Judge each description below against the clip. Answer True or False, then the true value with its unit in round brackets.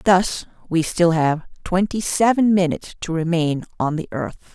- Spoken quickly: False (160 wpm)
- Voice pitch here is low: False (175 Hz)